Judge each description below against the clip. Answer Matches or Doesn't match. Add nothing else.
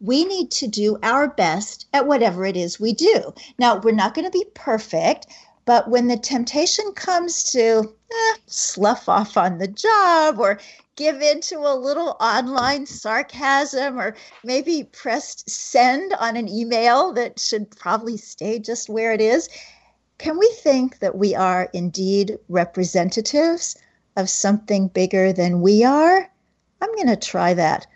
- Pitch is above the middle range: Matches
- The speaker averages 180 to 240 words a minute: Doesn't match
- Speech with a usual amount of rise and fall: Doesn't match